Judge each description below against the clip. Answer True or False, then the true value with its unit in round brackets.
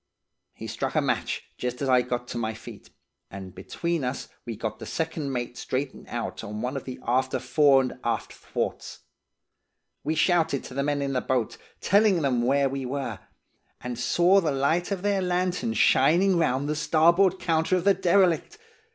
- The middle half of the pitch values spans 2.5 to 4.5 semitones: False (5.5 semitones)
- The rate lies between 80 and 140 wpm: False (185 wpm)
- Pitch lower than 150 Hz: True (140 Hz)